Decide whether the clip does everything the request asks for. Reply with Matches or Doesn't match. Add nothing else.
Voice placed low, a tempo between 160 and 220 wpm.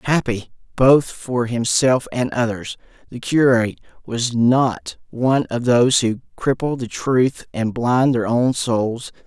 Doesn't match